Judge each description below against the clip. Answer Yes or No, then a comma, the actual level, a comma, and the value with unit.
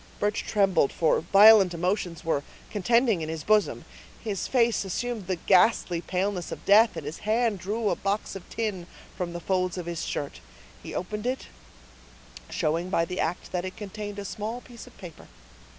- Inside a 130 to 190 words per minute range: Yes, average, 180 wpm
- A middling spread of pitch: Yes, average, 3.5 semitones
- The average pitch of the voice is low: No, high, 195 Hz